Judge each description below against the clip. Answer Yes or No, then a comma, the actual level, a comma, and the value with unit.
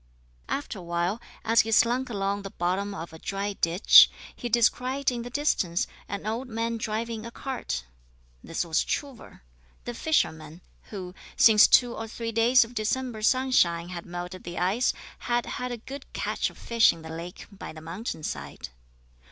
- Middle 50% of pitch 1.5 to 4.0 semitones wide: No, average, 5.3 semitones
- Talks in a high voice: Yes, high, 215 Hz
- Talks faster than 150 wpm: Yes, average, 175 wpm